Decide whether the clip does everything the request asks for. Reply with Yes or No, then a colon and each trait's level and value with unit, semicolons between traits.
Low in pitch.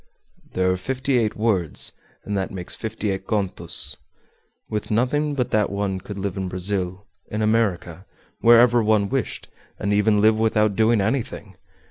Yes: low, 105 Hz